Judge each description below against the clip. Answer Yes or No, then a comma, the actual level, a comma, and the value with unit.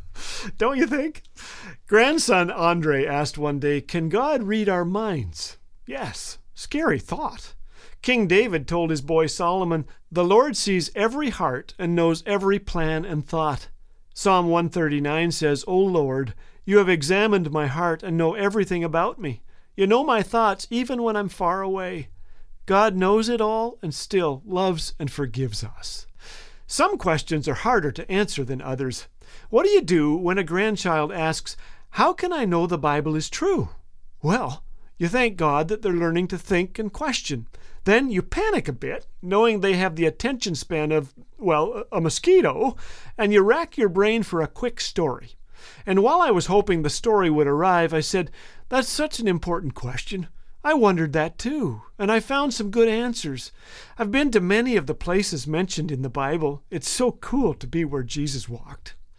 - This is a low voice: No, medium, 175 Hz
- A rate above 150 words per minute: Yes, average, 175 wpm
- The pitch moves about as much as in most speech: No, wide, 6.0 semitones